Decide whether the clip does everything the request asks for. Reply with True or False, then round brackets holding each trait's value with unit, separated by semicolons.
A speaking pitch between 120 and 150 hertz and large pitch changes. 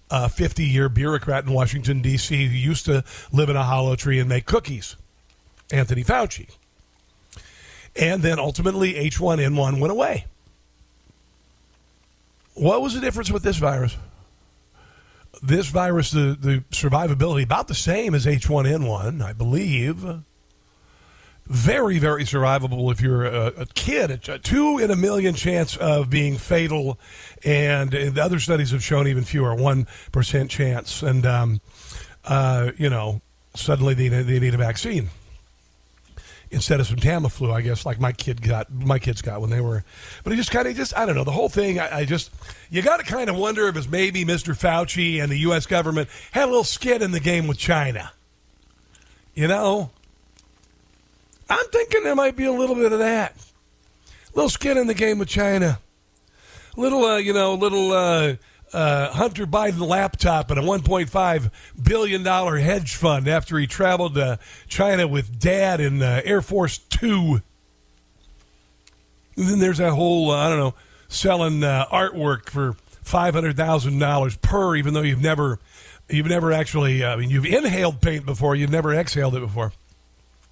True (140 Hz; 6.6 semitones)